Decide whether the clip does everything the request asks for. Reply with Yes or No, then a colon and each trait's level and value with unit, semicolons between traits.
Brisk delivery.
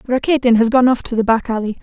Yes: fast, 265 wpm